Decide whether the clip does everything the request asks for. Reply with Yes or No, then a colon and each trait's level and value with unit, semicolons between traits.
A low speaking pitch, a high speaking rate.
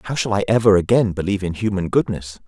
Yes: low, 100 Hz; fast, 220 wpm